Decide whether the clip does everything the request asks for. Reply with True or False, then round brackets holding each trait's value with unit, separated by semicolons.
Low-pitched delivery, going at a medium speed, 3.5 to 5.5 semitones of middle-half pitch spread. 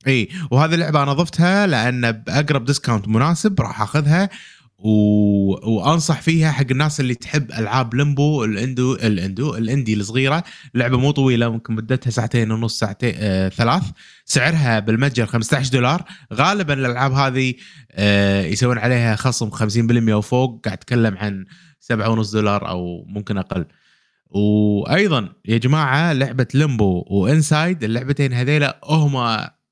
True (125 Hz; 125 wpm; 4.6 semitones)